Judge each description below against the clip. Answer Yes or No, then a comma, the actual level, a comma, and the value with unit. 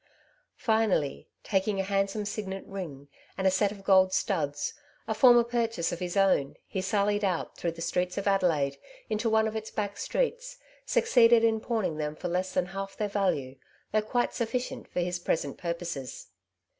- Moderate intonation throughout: Yes, average, 3.8 semitones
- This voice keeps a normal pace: Yes, average, 175 wpm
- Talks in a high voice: Yes, high, 195 Hz